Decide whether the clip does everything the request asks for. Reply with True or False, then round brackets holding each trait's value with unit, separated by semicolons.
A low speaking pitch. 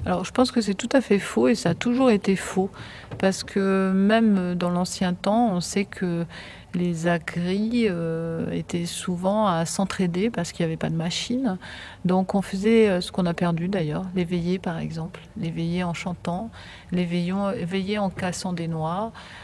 False (185 Hz)